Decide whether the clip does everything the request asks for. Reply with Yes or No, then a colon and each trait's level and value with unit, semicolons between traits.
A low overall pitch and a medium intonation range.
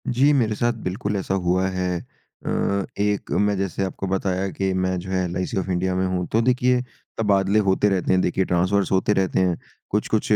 No: very low, 95 Hz; narrow, 1.8 semitones